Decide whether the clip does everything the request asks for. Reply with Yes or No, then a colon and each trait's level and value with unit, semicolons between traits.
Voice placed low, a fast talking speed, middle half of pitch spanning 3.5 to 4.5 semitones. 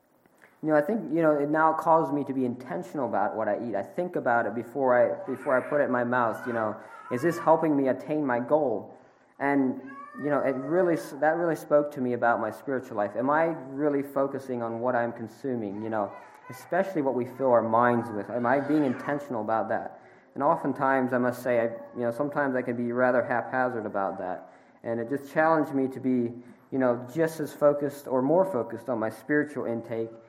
Yes: low, 130 Hz; fast, 220 wpm; average, 3.8 semitones